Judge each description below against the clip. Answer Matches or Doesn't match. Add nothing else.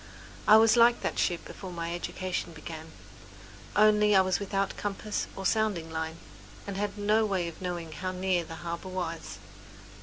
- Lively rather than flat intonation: Doesn't match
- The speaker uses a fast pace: Doesn't match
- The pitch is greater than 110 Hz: Matches